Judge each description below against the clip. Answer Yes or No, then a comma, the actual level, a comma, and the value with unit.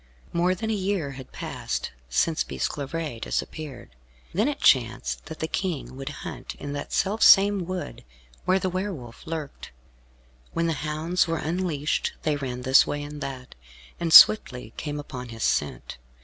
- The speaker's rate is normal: Yes, average, 165 wpm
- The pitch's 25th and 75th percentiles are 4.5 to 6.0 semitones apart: Yes, average, 5.1 semitones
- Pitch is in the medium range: Yes, medium, 155 Hz